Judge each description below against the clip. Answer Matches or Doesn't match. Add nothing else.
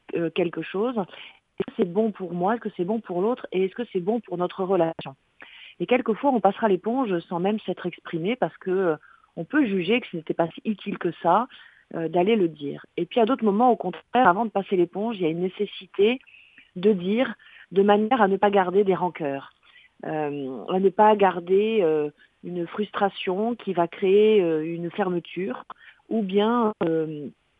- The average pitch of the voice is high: Matches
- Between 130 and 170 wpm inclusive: Doesn't match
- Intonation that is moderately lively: Matches